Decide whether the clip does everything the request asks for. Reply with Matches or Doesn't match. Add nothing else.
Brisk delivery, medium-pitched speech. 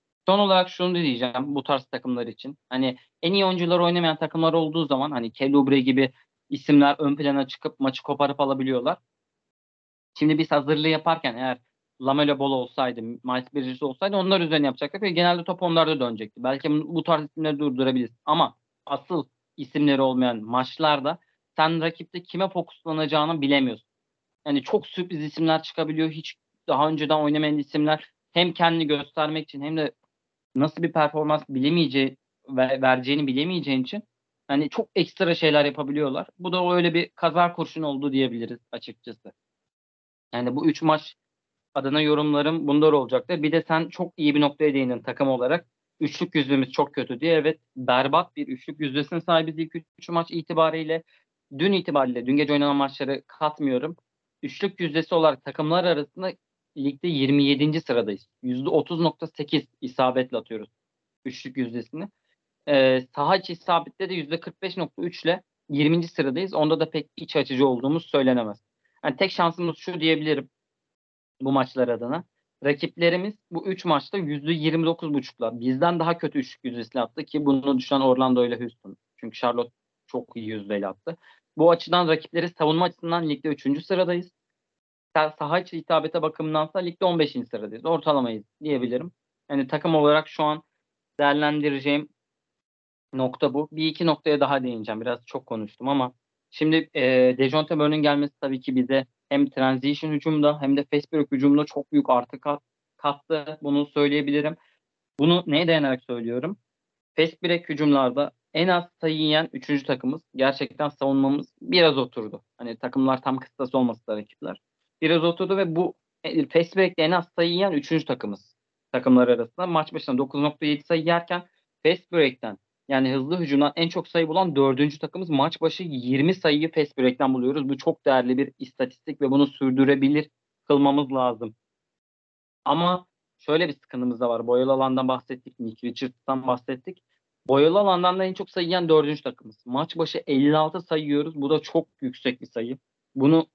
Matches